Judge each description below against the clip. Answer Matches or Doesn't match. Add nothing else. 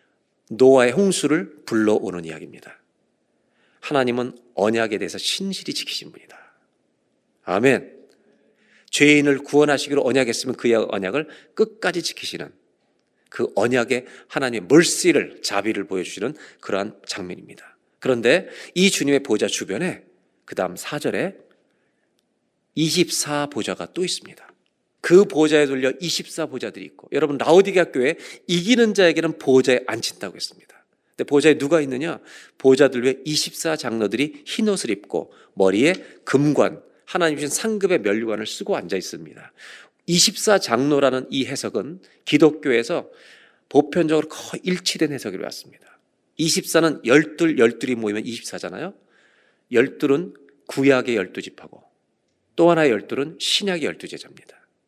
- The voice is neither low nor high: Matches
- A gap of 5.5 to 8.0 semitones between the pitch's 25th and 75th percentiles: Doesn't match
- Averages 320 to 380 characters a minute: Doesn't match